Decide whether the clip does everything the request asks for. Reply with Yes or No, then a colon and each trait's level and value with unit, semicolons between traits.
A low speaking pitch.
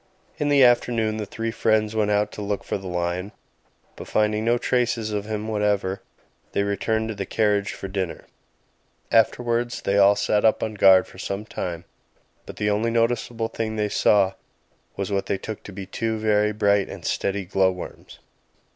Yes: low, 105 Hz